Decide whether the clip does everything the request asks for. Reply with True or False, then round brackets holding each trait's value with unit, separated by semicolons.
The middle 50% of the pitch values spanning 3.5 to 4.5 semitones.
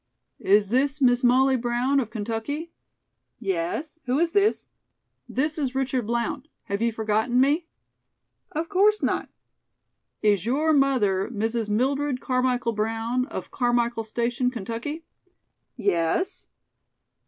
True (3.8 semitones)